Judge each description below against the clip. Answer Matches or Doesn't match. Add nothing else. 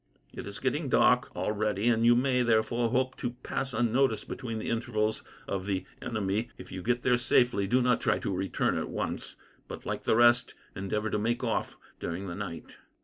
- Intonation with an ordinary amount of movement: Matches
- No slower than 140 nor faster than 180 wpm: Doesn't match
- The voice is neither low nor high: Doesn't match